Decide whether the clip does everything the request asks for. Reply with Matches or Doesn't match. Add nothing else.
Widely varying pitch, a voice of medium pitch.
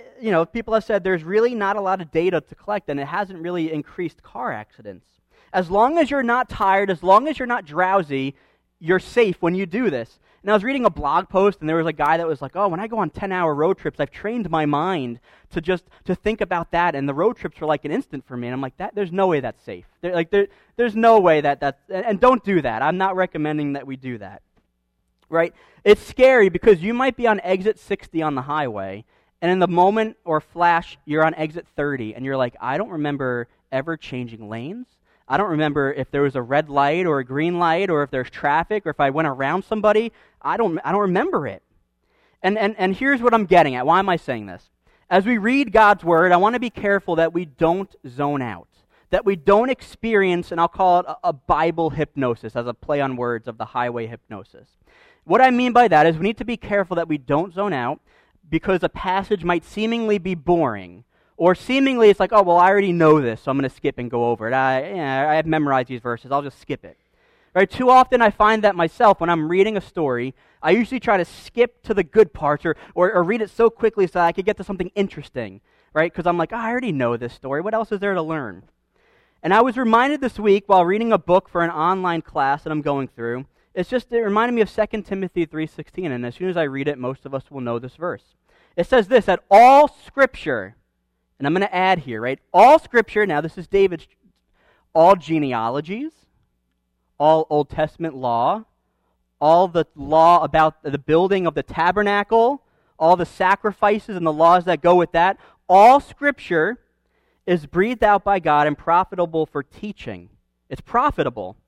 Matches